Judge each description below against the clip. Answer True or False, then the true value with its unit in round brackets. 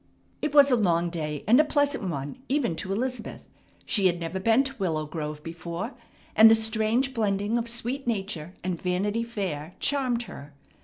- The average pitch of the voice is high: True (210 Hz)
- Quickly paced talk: False (175 wpm)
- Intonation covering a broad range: True (5.9 semitones)